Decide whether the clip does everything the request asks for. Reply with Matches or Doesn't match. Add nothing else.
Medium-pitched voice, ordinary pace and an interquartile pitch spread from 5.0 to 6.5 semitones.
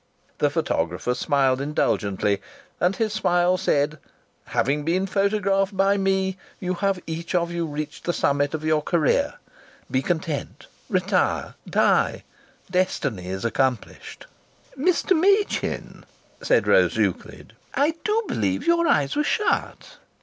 Doesn't match